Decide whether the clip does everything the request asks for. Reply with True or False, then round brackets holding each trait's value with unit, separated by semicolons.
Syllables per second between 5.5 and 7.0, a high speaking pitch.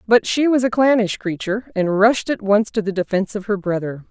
True (5.7 syllables/s; 210 Hz)